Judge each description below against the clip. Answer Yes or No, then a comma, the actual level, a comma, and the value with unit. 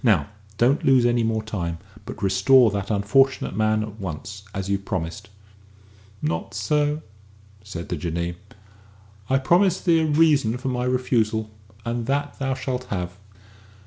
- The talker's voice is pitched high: No, low, 110 Hz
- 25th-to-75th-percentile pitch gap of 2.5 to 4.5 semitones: No, average, 5.3 semitones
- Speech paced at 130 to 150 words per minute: Yes, average, 145 wpm